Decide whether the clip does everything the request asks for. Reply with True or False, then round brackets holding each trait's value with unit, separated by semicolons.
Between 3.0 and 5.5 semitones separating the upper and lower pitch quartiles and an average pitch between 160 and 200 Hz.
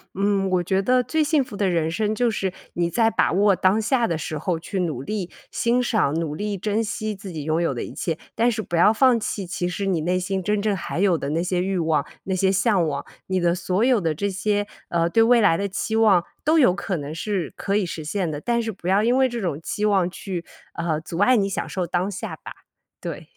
True (3.8 semitones; 195 Hz)